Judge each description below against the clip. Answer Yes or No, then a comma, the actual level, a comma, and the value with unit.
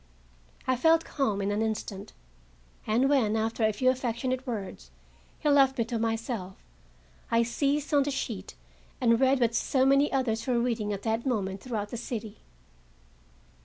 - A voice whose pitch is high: Yes, high, 235 Hz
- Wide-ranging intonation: No, average, 3.3 semitones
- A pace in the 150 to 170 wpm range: Yes, average, 165 wpm